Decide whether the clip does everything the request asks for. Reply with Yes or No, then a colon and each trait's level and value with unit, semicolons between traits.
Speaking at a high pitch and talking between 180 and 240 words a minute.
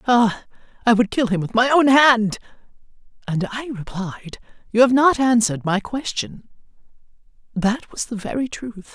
No: high, 230 Hz; average, 155 wpm